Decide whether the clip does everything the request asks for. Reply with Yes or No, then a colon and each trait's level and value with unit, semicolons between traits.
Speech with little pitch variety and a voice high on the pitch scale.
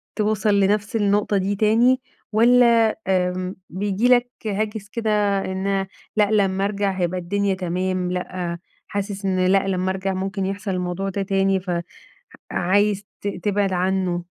Yes: narrow, 1.8 semitones; high, 195 Hz